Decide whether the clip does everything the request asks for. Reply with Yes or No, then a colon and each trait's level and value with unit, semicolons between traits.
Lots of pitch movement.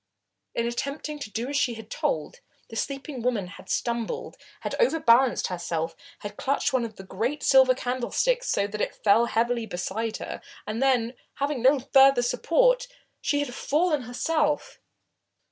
No: average, 4.1 semitones